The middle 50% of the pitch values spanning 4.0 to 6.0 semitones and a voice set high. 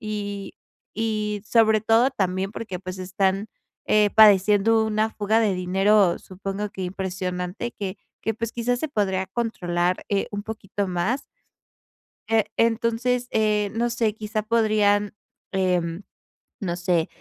No: average, 2.7 semitones; high, 210 Hz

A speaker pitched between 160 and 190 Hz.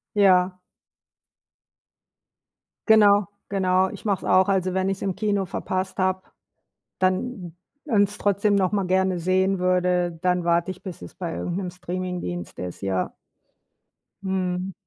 Yes: medium, 185 Hz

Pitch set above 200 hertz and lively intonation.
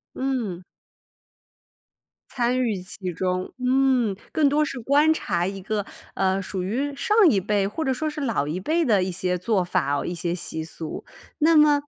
Yes: high, 210 Hz; wide, 7.1 semitones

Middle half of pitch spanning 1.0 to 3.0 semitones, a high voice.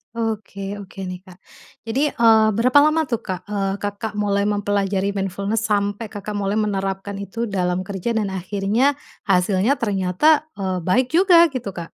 Yes: narrow, 2.4 semitones; high, 200 Hz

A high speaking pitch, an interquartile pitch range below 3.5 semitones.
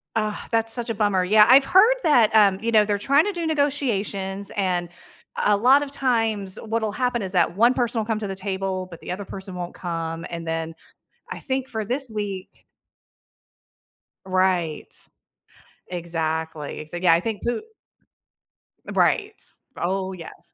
No: high, 205 Hz; average, 4.4 semitones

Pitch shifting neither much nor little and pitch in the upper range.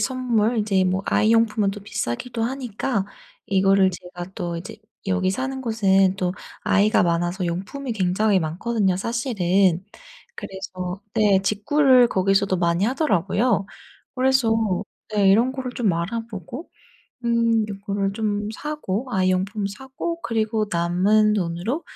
Yes: average, 3.8 semitones; high, 205 Hz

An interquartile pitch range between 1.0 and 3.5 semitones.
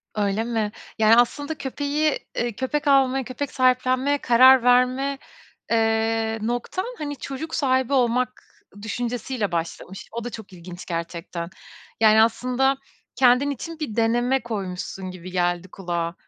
No: average, 3.9 semitones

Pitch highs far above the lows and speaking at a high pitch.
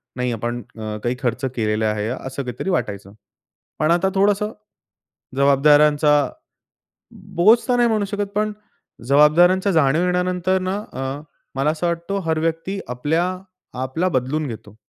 No: wide, 6.4 semitones; medium, 155 Hz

